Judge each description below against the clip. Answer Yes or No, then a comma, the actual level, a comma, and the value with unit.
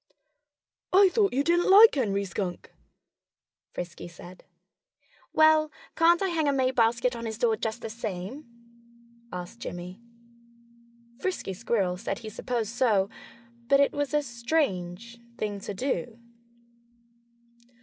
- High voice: Yes, high, 235 Hz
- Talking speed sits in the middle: No, slow, 130 wpm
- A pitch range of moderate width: No, wide, 6.6 semitones